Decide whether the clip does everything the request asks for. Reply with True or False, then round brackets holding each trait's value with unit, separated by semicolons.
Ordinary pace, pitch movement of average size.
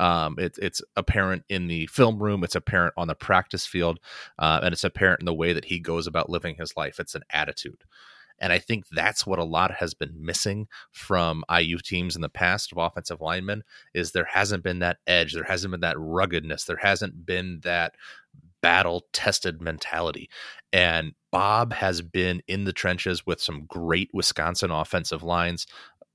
False (185 wpm; 2.0 semitones)